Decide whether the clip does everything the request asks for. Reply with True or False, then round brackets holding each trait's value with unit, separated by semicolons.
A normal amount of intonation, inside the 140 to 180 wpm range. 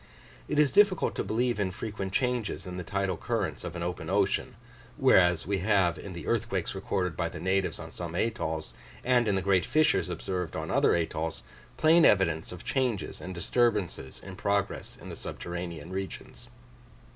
True (4.0 semitones; 175 wpm)